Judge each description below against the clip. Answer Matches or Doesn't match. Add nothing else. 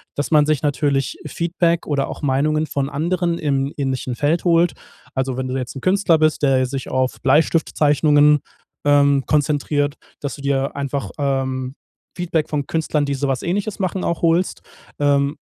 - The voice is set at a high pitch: Doesn't match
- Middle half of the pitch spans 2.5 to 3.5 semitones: Matches